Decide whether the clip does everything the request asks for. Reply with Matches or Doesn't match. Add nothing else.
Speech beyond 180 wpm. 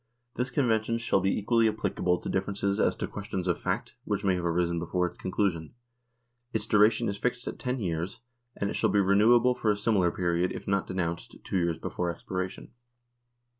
Matches